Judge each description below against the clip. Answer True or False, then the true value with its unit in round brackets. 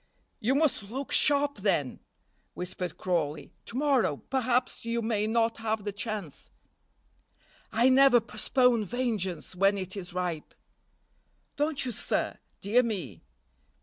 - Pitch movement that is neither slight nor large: True (5.0 semitones)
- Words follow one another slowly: True (125 wpm)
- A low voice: False (220 Hz)